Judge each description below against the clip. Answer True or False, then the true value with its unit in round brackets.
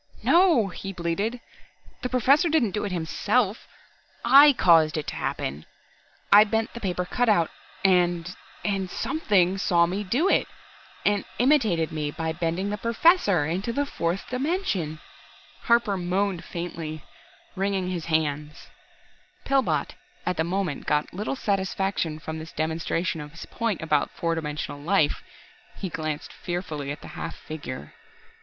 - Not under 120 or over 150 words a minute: True (140 wpm)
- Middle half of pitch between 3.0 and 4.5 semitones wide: False (5.0 semitones)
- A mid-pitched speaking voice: True (180 Hz)